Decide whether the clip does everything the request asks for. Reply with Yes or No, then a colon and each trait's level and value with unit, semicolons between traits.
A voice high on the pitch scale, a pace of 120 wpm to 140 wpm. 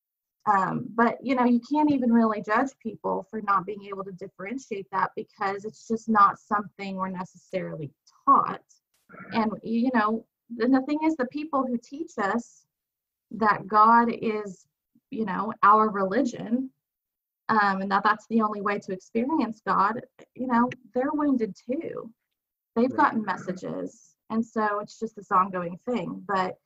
No: high, 220 Hz; average, 160 wpm